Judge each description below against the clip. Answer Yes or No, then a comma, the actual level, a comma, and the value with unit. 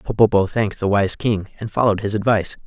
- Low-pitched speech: Yes, low, 105 Hz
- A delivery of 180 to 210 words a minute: Yes, average, 200 wpm